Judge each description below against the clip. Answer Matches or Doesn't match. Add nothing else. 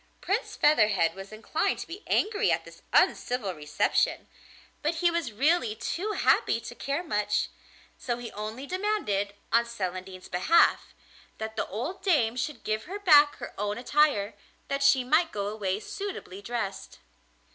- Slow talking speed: Doesn't match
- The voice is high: Matches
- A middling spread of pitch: Doesn't match